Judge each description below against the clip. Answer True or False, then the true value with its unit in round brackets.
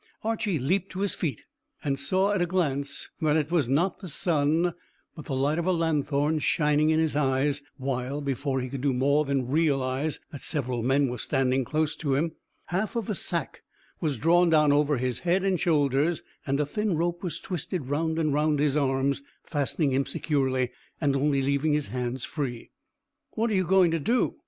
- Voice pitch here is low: False (150 Hz)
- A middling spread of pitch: True (3.6 semitones)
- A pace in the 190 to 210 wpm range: True (195 wpm)